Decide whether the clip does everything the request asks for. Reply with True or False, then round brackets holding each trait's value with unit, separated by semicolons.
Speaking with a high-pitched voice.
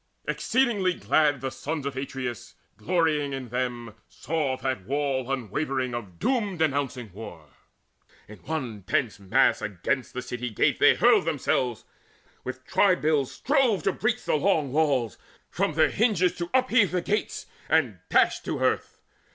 False (140 Hz)